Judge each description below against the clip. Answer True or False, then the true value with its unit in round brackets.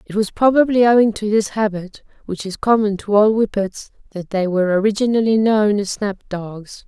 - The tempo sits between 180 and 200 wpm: True (185 wpm)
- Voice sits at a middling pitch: False (210 Hz)